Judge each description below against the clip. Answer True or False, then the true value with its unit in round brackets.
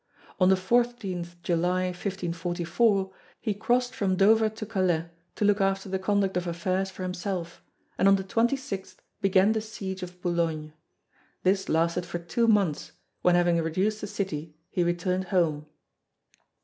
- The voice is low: False (185 Hz)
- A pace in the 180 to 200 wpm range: False (150 wpm)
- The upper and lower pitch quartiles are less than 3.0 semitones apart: True (2.6 semitones)